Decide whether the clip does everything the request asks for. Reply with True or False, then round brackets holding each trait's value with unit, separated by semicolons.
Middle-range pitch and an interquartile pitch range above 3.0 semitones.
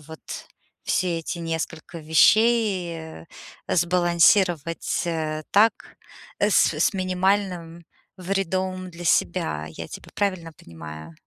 False (170 Hz; 2.7 semitones)